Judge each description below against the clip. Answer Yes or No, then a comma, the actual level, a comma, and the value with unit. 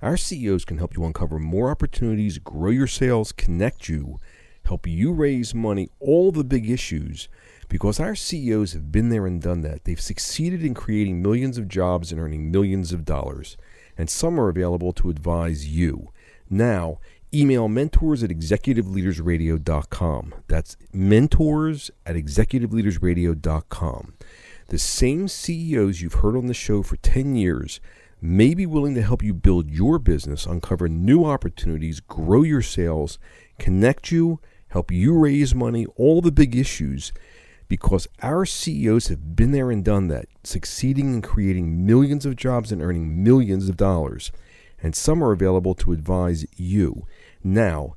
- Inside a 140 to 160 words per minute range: Yes, average, 155 wpm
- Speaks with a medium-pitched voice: No, very low, 95 Hz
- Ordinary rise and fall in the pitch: No, wide, 6.6 semitones